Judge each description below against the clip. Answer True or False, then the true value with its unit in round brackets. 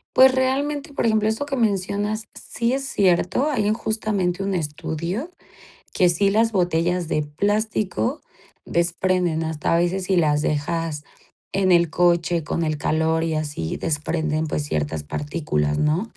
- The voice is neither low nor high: True (175 Hz)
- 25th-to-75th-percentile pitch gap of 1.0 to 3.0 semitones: False (5.2 semitones)